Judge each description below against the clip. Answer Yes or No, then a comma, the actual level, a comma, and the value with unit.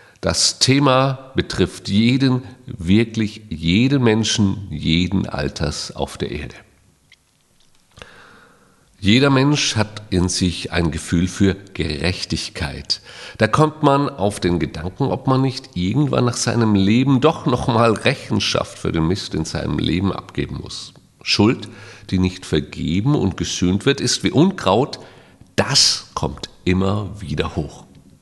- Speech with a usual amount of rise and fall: No, wide, 5.7 semitones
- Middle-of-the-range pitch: No, low, 105 Hz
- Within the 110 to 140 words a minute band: Yes, average, 130 wpm